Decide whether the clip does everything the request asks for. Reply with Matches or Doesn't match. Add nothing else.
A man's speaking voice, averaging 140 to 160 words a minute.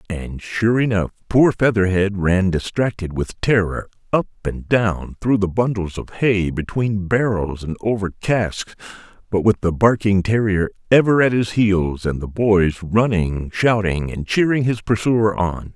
Matches